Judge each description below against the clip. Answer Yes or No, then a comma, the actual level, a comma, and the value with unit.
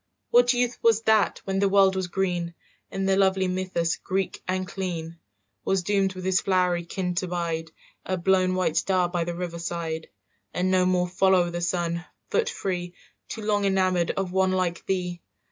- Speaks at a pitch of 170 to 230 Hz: Yes, medium, 185 Hz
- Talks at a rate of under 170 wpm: No, average, 180 wpm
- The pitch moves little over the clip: Yes, narrow, 1.7 semitones